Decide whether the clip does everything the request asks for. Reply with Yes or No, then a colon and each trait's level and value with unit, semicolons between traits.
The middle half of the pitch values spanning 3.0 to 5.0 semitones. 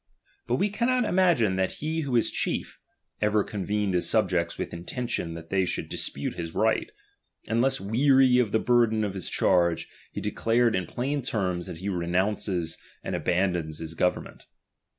No: wide, 5.6 semitones